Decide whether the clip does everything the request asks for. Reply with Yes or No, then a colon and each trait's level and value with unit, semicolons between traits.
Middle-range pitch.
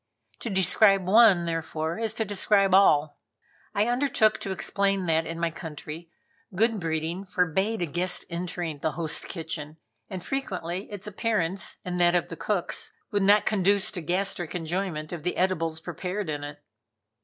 Yes: medium, 180 Hz